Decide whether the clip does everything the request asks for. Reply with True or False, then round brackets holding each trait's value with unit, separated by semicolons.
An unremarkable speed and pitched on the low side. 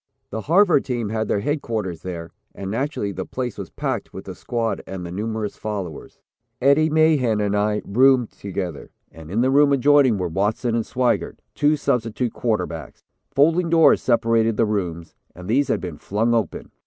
True (175 wpm; 115 Hz)